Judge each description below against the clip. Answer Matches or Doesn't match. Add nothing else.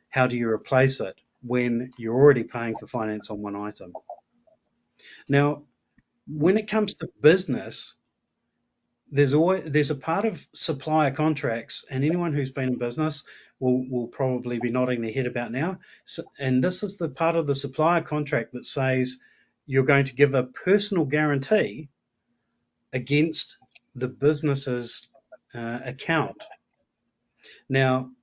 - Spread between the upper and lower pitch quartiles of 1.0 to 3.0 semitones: Doesn't match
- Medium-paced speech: Matches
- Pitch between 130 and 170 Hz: Matches